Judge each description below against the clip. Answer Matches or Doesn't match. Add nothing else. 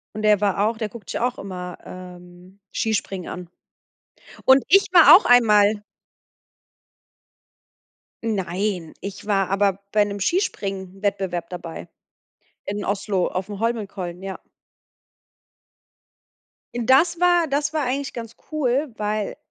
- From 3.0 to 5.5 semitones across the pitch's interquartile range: Matches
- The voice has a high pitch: Matches